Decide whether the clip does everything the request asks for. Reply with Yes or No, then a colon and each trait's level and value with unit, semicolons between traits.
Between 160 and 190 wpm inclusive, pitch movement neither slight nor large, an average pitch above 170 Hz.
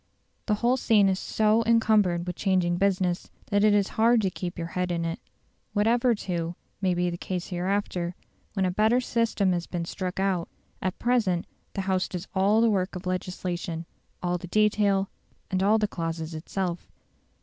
Yes: average, 180 wpm; average, 3.0 semitones; high, 190 Hz